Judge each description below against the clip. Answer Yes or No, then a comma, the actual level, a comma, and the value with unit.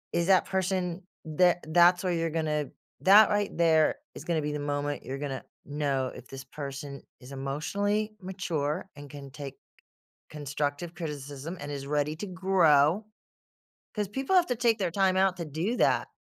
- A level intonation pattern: No, average, 4.6 semitones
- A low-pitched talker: No, medium, 160 Hz